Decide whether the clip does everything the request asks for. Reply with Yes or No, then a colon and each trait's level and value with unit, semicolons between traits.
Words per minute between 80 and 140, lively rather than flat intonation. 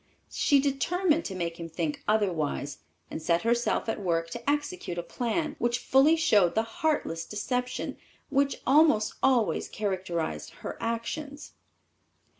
Yes: slow, 135 wpm; wide, 8.4 semitones